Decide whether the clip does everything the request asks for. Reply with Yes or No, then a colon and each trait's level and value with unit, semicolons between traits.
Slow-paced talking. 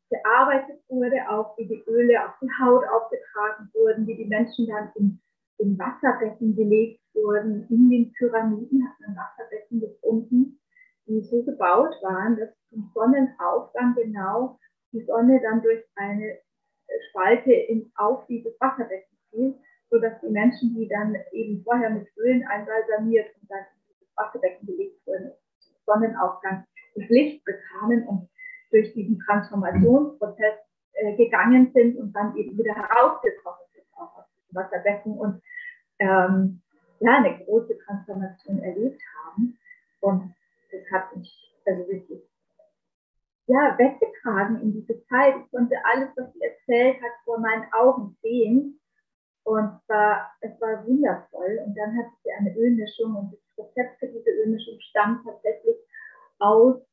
No: average, 140 wpm